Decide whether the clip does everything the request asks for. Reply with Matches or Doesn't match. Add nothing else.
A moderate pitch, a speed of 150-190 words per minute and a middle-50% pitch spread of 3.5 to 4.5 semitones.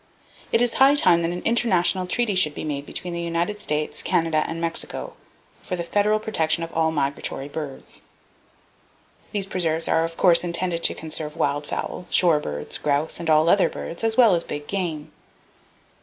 Doesn't match